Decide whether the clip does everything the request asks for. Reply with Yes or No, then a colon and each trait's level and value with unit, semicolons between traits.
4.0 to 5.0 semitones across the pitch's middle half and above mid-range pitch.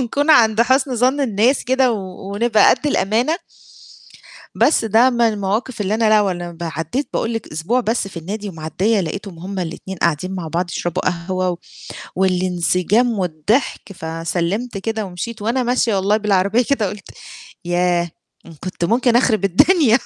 Yes: average, 4.6 semitones; high, 205 Hz